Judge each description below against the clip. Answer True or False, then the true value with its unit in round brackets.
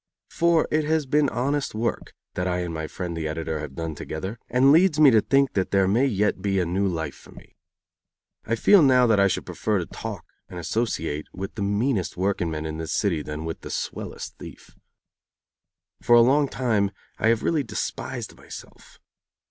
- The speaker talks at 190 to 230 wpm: True (195 wpm)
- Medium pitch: False (100 Hz)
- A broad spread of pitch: True (7.3 semitones)